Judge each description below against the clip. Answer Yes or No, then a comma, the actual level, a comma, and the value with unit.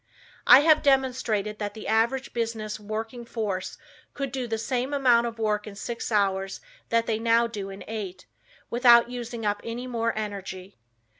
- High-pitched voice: Yes, high, 225 Hz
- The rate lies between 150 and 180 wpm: Yes, average, 165 wpm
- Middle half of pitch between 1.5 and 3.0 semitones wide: Yes, narrow, 2.4 semitones